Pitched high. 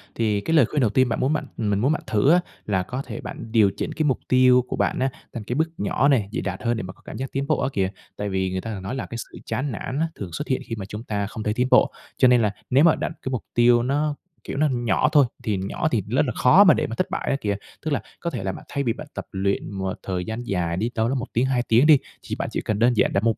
No: low, 120 Hz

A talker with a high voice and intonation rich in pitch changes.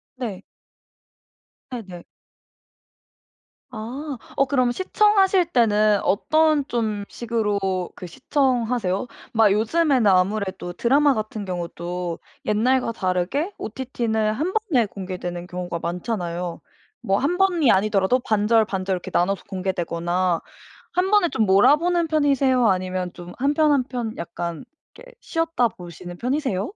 Yes: high, 220 Hz; wide, 6.8 semitones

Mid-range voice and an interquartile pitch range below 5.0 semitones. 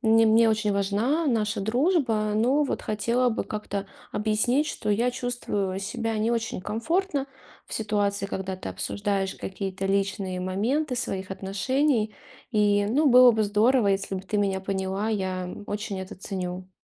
No: high, 210 Hz; average, 3.4 semitones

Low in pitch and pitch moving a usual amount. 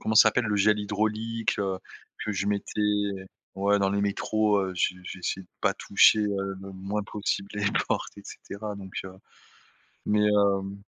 No: low, 100 Hz; narrow, 1.3 semitones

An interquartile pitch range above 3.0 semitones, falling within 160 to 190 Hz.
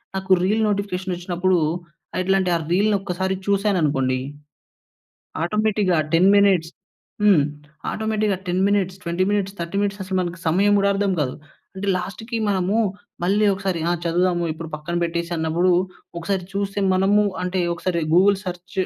No: narrow, 2.4 semitones; medium, 185 Hz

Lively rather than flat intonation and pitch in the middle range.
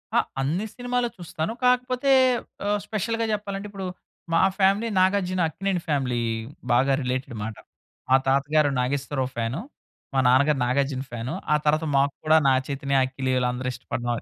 Yes: wide, 7.0 semitones; medium, 145 Hz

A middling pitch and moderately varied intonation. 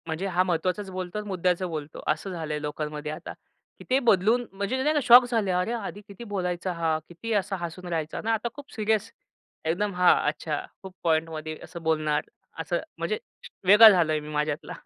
Yes: medium, 180 Hz; average, 4.7 semitones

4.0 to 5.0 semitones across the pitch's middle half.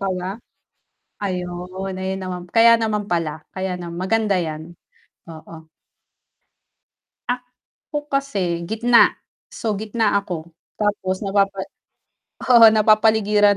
No: average, 3.3 semitones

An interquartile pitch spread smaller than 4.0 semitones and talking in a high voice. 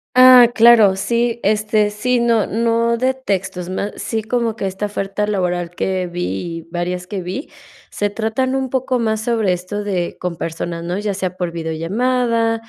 No: average, 4.3 semitones; high, 210 Hz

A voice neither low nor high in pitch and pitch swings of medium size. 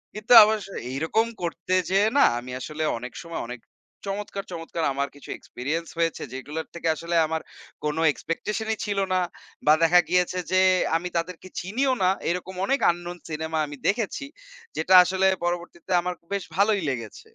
Yes: medium, 175 Hz; average, 3.5 semitones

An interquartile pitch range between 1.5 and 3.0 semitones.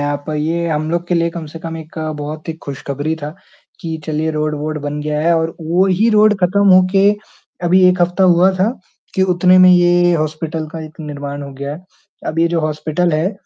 Yes: narrow, 2.6 semitones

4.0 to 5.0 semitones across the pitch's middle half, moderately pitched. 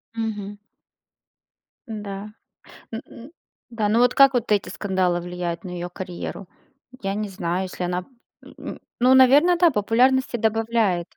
No: average, 4.6 semitones; high, 210 Hz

